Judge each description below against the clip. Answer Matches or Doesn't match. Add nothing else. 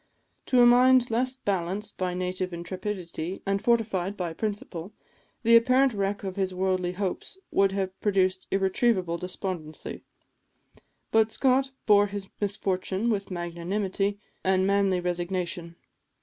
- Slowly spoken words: Matches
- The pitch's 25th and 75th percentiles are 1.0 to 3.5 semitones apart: Matches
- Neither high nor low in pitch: Doesn't match